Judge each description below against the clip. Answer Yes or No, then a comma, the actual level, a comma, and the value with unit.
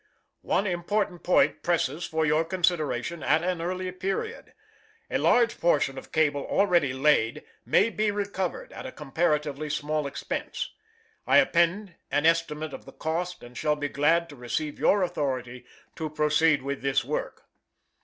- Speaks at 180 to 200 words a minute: No, average, 155 wpm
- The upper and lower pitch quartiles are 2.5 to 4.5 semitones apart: Yes, average, 3.7 semitones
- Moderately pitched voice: Yes, medium, 160 Hz